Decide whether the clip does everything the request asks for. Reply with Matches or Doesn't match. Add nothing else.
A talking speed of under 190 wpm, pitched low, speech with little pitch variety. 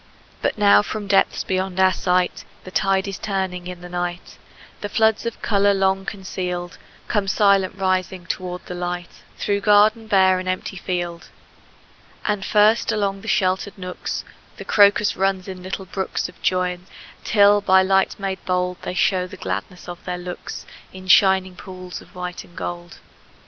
Doesn't match